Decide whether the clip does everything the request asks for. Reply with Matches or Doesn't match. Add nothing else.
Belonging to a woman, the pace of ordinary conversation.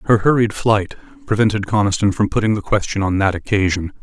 Doesn't match